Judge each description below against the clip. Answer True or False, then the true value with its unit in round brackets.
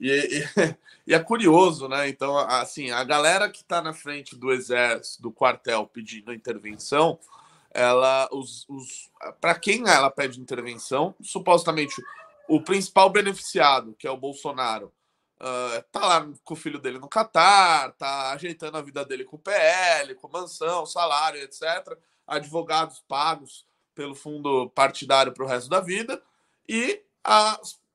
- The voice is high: False (150 Hz)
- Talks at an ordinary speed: True (145 wpm)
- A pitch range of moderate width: False (5.7 semitones)